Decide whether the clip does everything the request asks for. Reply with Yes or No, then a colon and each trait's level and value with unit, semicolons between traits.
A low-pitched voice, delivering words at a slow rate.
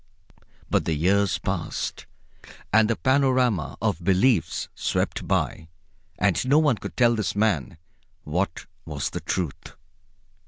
Yes: low, 100 Hz; slow, 125 wpm